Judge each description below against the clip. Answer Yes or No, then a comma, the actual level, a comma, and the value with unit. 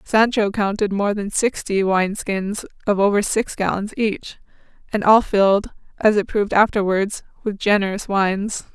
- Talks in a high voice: Yes, high, 205 Hz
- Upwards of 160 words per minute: No, average, 150 wpm